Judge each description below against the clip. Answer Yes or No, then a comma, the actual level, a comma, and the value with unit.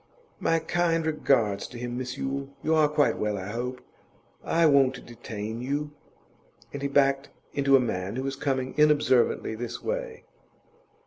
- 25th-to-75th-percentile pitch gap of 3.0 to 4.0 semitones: Yes, average, 3.6 semitones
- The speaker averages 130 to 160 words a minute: Yes, average, 155 wpm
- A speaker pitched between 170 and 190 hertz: No, low, 135 Hz